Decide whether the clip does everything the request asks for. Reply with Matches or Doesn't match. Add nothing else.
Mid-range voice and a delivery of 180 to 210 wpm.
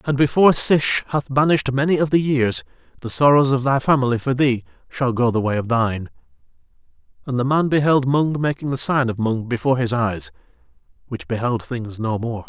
Doesn't match